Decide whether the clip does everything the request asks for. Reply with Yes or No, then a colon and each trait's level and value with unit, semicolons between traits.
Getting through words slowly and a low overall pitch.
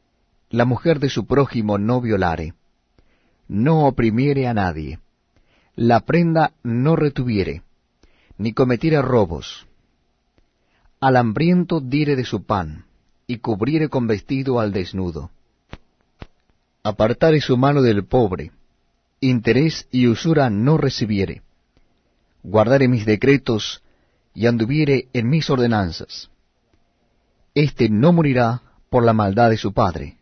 Yes: slow, 115 wpm; low, 120 Hz